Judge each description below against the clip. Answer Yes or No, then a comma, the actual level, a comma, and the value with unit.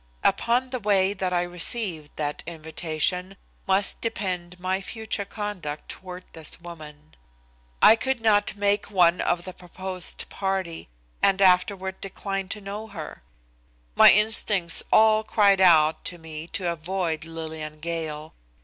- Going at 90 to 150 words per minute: Yes, slow, 135 wpm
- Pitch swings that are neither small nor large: Yes, average, 3.6 semitones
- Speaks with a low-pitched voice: No, medium, 185 Hz